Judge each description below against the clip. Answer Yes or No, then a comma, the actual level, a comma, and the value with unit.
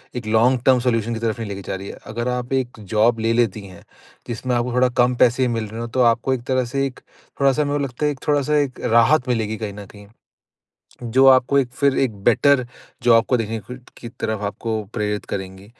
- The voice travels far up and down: No, average, 2.7 semitones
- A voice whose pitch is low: Yes, low, 120 Hz